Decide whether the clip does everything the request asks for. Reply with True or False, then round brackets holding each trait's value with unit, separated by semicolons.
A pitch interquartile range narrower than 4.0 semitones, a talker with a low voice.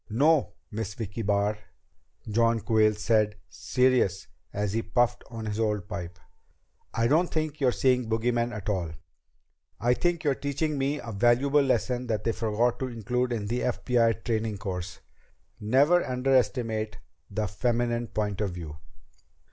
True (3.2 semitones; 115 Hz)